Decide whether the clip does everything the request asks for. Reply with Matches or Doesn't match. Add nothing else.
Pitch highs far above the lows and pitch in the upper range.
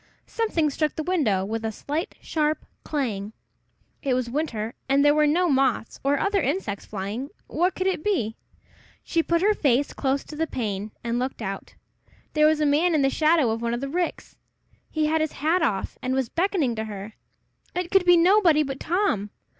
Matches